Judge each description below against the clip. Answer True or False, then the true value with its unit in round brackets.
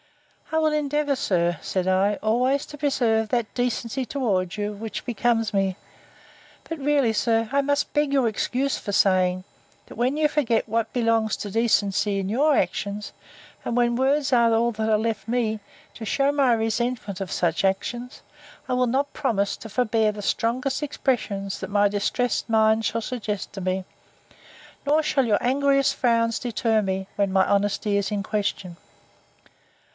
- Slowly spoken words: False (165 wpm)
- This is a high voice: True (225 Hz)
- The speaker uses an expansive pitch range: False (3.9 semitones)